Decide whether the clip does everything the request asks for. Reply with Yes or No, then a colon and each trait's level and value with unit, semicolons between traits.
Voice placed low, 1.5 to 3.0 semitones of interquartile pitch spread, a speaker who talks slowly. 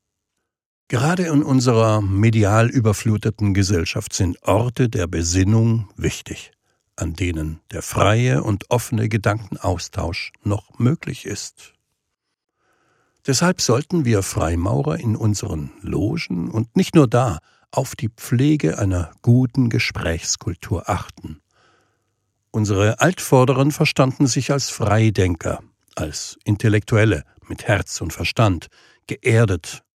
No: low, 110 Hz; average, 4.3 semitones; slow, 105 wpm